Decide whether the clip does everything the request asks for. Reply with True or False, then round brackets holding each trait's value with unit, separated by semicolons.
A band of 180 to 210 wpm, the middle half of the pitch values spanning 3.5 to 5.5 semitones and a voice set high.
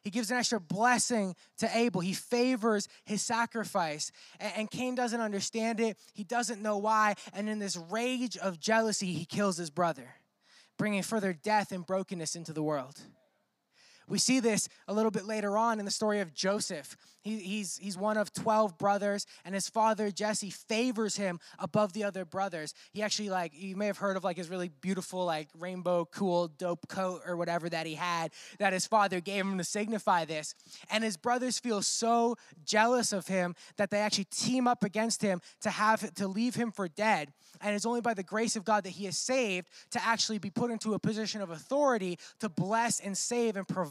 False (200 wpm; 3.1 semitones; 205 Hz)